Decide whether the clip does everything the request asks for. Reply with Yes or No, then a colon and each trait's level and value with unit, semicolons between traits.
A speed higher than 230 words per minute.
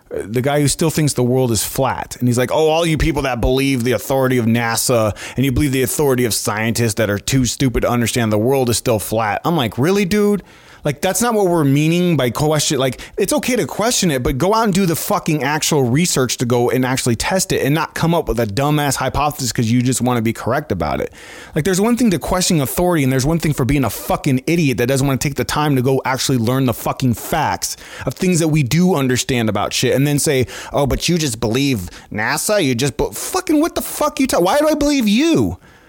Yes: fast, 255 wpm